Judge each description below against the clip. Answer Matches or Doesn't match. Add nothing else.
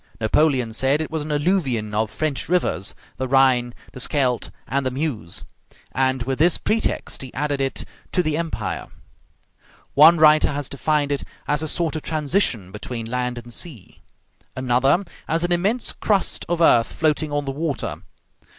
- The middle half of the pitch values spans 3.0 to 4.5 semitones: Matches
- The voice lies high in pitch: Doesn't match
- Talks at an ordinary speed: Matches